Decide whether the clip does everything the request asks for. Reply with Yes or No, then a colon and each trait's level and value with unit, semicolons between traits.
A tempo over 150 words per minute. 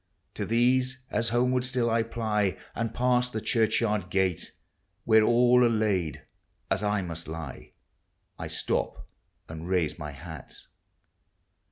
No: slow, 135 wpm